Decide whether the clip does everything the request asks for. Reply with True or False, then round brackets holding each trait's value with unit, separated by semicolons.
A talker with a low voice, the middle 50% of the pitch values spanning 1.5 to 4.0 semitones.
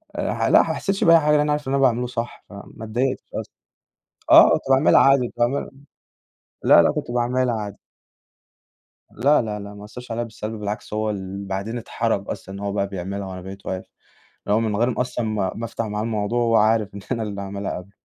True (110 Hz; 3.3 semitones)